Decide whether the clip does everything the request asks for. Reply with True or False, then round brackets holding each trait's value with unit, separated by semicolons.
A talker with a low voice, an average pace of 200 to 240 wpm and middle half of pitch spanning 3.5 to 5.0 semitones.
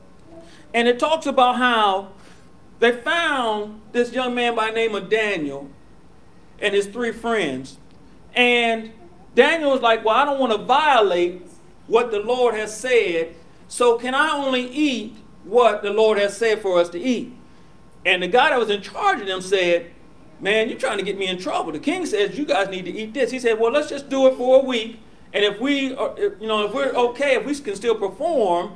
False (230 Hz; 205 wpm; 4.2 semitones)